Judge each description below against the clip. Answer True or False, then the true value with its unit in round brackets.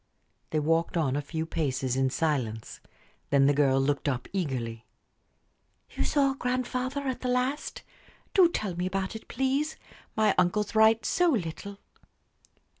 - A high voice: False (180 Hz)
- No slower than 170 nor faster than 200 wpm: False (145 wpm)